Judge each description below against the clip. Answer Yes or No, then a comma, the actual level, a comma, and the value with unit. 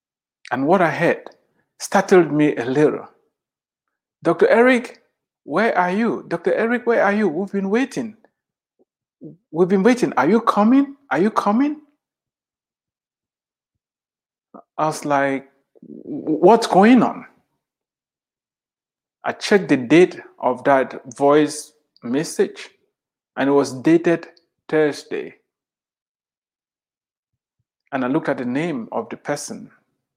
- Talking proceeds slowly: Yes, slow, 115 wpm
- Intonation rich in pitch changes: Yes, wide, 8.3 semitones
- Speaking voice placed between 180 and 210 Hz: Yes, high, 190 Hz